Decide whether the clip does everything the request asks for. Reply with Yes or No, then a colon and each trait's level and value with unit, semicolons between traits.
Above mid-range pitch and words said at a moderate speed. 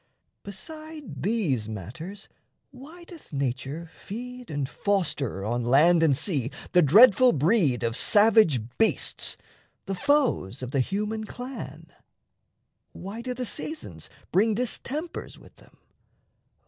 No: high, 195 Hz; slow, 120 wpm